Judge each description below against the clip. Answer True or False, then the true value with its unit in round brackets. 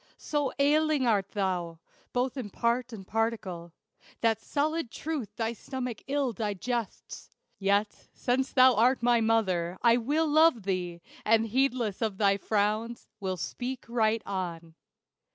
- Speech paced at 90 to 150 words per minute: True (135 wpm)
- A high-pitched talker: True (225 Hz)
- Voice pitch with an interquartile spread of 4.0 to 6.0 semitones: True (4.4 semitones)